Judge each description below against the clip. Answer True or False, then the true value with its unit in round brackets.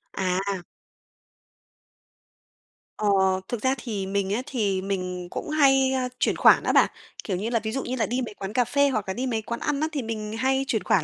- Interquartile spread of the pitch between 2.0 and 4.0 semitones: False (4.8 semitones)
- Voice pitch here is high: True (220 Hz)